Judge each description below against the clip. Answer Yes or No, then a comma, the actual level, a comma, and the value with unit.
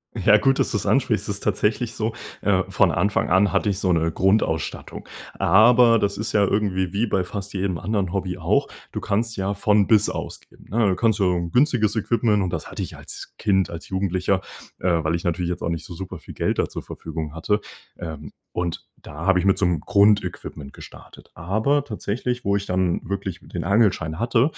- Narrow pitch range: No, average, 3.2 semitones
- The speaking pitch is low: Yes, low, 100 Hz